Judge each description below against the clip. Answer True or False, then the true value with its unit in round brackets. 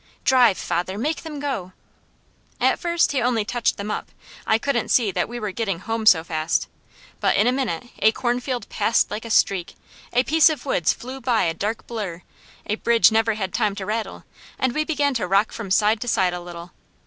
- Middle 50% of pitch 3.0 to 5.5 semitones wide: True (4.5 semitones)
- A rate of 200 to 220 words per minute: True (205 wpm)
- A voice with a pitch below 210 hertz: False (225 Hz)